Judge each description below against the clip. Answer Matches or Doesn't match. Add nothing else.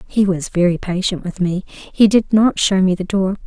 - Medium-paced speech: Doesn't match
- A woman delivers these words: Matches